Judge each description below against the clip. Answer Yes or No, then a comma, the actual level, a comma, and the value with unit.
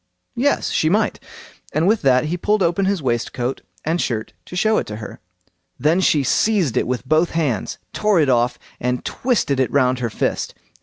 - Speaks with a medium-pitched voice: Yes, medium, 155 Hz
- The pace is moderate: Yes, average, 185 wpm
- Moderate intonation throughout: No, wide, 7.0 semitones